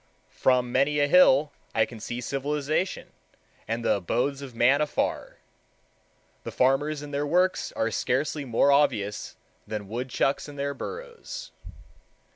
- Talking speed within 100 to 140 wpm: Yes, slow, 135 wpm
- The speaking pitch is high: No, medium, 140 Hz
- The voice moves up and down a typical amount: Yes, average, 3.4 semitones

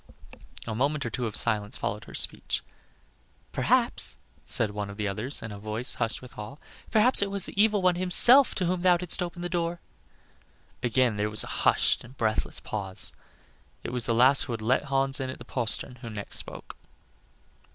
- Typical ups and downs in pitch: No, wide, 8.2 semitones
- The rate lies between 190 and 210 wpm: Yes, average, 195 wpm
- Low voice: Yes, low, 125 Hz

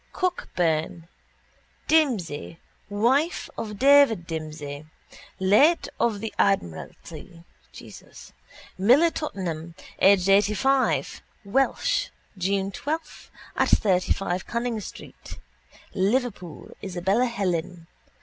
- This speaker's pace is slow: Yes, slow, 80 wpm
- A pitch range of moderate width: No, wide, 6.0 semitones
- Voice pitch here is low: No, high, 195 Hz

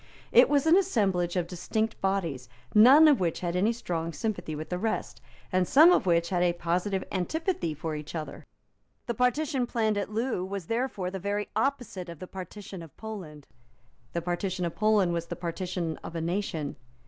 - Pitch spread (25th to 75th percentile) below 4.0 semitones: No, average, 4.4 semitones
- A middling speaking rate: Yes, average, 185 wpm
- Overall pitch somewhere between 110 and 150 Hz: No, medium, 185 Hz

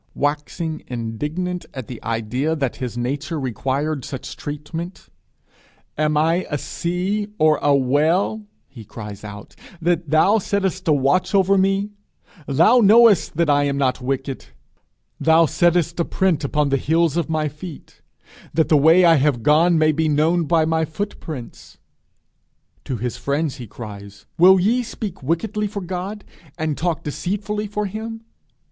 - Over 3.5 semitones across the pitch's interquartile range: Yes, average, 4.6 semitones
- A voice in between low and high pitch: Yes, medium, 160 Hz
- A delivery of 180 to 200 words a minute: No, average, 155 wpm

